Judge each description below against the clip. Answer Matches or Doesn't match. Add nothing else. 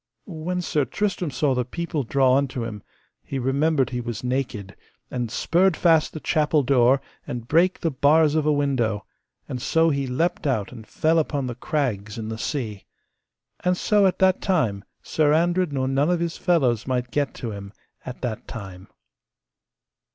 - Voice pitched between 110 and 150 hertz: Matches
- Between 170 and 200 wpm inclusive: Matches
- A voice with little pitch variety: Doesn't match